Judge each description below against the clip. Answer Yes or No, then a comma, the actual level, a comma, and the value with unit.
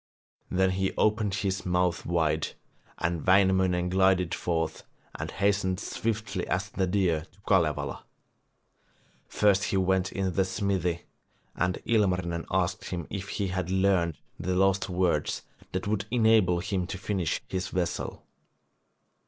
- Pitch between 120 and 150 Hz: No, very low, 95 Hz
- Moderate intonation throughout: No, narrow, 1.8 semitones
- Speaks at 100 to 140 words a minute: Yes, slow, 135 wpm